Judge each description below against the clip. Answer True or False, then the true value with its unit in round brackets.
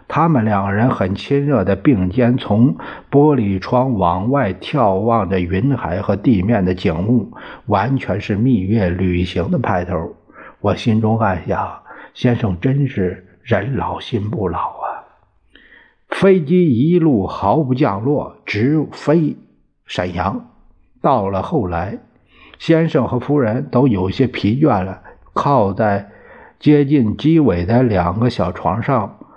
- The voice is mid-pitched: False (115 Hz)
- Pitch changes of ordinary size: False (6.1 semitones)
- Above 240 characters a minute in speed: False (185 characters per minute)